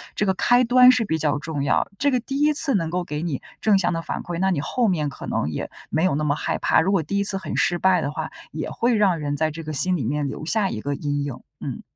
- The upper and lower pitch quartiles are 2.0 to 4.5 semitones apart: No, wide, 5.4 semitones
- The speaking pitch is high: No, medium, 170 Hz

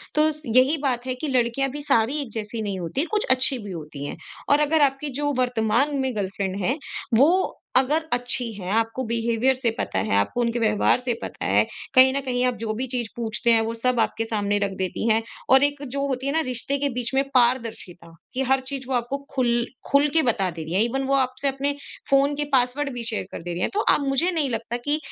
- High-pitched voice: Yes, very high, 250 Hz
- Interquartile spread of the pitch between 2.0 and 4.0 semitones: Yes, average, 3.6 semitones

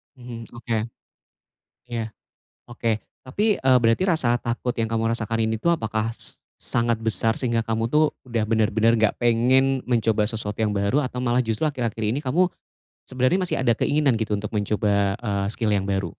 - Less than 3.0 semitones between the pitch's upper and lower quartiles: Yes, narrow, 2.5 semitones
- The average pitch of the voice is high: No, low, 115 Hz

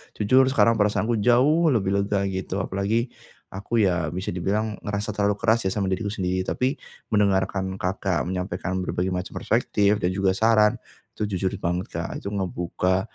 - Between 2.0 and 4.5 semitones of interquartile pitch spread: Yes, narrow, 2.5 semitones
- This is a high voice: No, low, 100 Hz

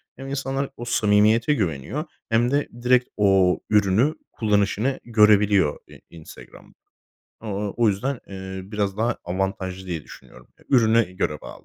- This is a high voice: No, low, 105 Hz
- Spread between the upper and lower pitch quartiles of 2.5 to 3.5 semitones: No, average, 3.9 semitones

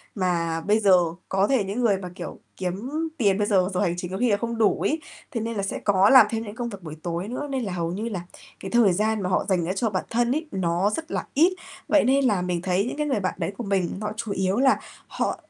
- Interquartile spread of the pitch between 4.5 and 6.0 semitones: No, average, 4.1 semitones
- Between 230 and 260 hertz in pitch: No, high, 205 Hz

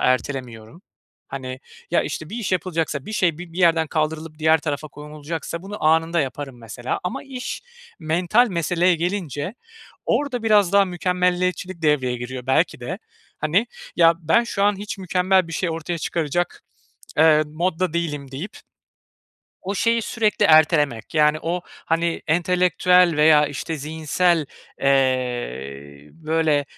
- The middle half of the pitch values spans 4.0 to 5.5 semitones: No, average, 3.6 semitones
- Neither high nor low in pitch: Yes, medium, 165 Hz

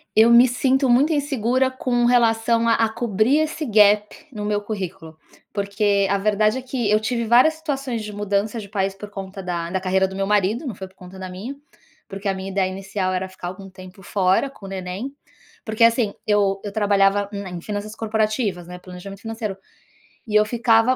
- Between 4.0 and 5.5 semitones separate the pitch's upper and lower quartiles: No, average, 3.3 semitones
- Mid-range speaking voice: No, high, 210 Hz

